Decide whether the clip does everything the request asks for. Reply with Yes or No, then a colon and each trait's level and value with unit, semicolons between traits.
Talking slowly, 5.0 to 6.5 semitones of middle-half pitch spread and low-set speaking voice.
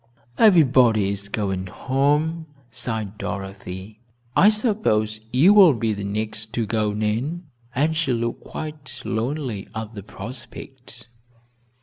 Yes: slow, 120 wpm; wide, 5.5 semitones; low, 115 Hz